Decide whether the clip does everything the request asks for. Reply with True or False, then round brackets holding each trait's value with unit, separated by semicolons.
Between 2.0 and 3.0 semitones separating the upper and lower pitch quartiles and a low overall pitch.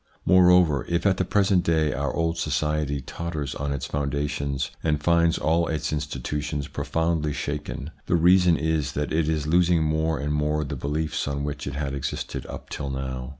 True (2.6 semitones; 75 Hz)